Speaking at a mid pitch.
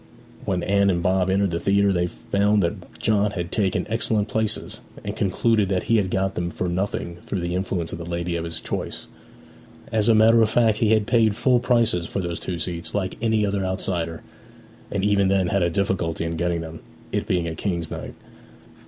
No: very low, 95 Hz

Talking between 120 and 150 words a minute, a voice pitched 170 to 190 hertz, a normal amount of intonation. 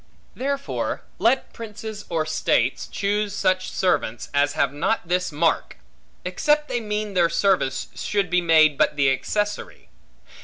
Yes: average, 140 wpm; medium, 185 Hz; average, 5.0 semitones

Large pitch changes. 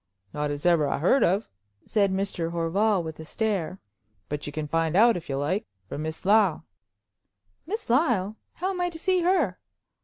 Yes: wide, 6.3 semitones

